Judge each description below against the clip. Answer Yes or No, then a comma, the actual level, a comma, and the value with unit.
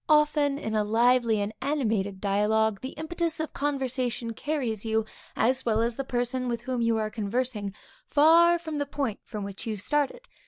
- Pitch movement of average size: Yes, average, 4.7 semitones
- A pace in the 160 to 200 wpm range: Yes, average, 180 wpm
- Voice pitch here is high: Yes, high, 245 Hz